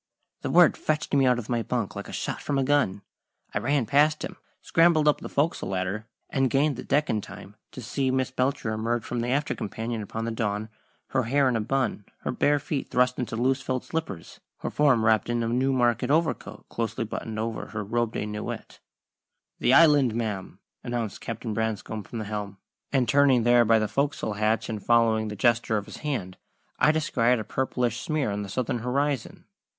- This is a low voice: Yes, low, 120 Hz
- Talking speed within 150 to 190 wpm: No, average, 200 wpm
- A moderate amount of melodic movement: Yes, average, 3.7 semitones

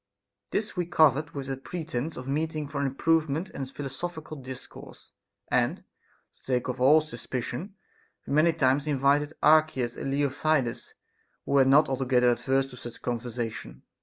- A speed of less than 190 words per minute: Yes, average, 150 wpm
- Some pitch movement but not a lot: Yes, average, 3.2 semitones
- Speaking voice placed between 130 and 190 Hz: Yes, medium, 140 Hz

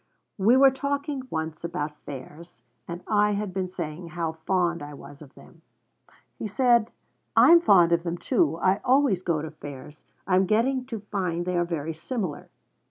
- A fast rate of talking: No, average, 180 wpm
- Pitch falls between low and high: Yes, medium, 180 Hz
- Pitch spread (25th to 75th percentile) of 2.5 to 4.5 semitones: No, average, 5.3 semitones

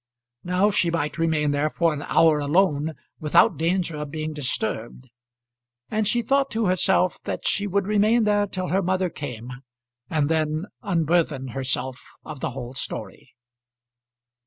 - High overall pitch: No, medium, 160 Hz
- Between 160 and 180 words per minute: No, average, 150 wpm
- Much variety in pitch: No, average, 4.6 semitones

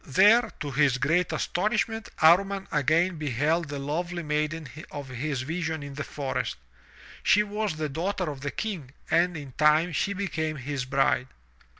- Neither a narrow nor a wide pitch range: Yes, average, 4.0 semitones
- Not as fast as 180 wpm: Yes, average, 160 wpm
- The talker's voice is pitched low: No, medium, 155 Hz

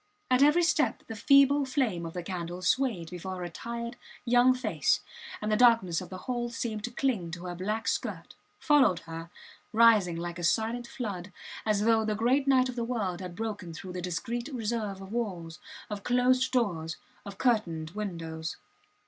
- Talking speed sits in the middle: Yes, average, 180 wpm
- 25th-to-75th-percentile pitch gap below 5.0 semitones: No, wide, 5.4 semitones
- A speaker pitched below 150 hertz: No, high, 215 Hz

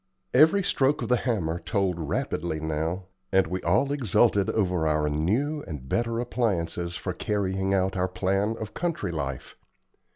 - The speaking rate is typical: Yes, average, 155 wpm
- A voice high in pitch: No, very low, 95 Hz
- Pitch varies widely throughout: Yes, wide, 5.7 semitones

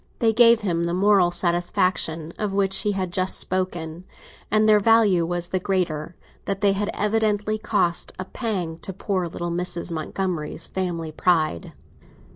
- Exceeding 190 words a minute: No, average, 155 wpm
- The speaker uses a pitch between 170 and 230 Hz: Yes, medium, 185 Hz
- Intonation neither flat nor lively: Yes, average, 3.1 semitones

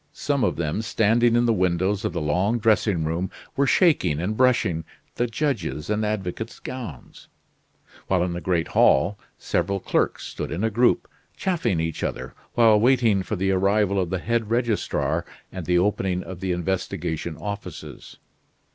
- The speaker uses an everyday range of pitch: Yes, average, 4.5 semitones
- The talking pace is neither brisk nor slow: Yes, average, 165 wpm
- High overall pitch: No, low, 100 Hz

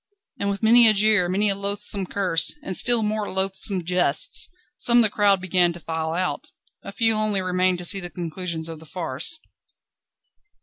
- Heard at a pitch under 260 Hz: Yes, high, 190 Hz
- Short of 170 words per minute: No, average, 185 wpm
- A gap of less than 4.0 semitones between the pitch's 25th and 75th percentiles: Yes, average, 3.0 semitones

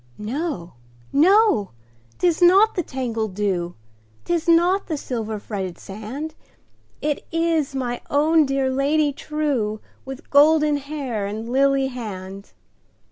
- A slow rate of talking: Yes, slow, 105 wpm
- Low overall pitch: No, very high, 270 Hz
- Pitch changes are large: Yes, wide, 6.5 semitones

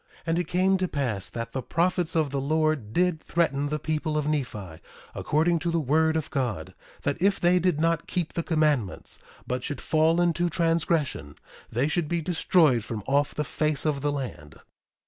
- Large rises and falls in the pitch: No, average, 3.5 semitones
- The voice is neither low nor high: Yes, medium, 155 Hz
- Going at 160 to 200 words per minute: Yes, average, 190 wpm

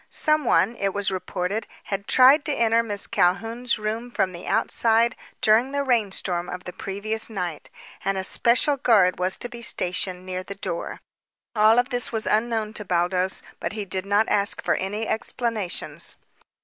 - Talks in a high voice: Yes, high, 210 Hz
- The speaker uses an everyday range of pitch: Yes, average, 3.7 semitones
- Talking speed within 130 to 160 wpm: No, average, 170 wpm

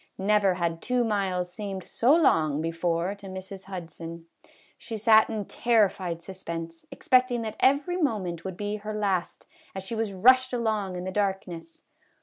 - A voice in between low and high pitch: No, high, 195 Hz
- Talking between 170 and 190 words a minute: No, average, 155 wpm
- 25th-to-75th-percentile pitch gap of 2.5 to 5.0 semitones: Yes, average, 3.8 semitones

